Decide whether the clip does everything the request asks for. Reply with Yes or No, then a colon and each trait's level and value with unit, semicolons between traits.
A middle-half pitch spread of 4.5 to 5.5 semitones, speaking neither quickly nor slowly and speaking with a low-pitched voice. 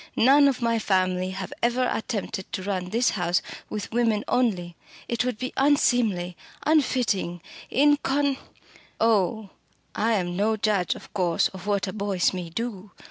No: average, 4.8 semitones; average, 155 wpm; high, 210 Hz